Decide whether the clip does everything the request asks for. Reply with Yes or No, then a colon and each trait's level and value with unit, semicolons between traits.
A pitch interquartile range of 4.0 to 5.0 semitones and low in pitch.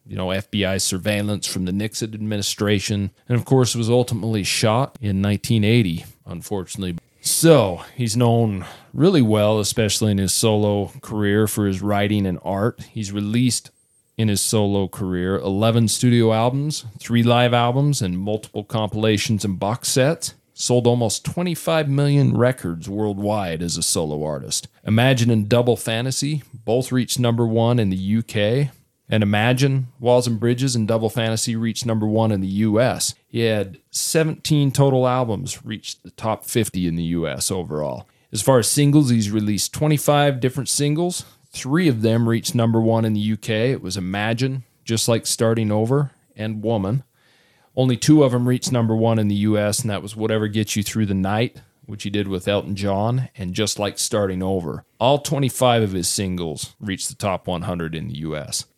No: average, 3.5 semitones; low, 115 Hz